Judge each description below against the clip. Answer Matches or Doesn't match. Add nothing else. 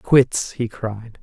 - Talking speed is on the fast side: Doesn't match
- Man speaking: Matches